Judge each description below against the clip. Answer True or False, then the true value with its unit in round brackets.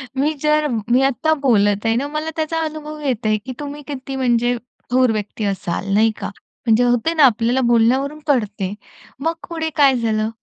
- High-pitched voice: True (255 Hz)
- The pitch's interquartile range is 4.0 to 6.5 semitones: True (4.8 semitones)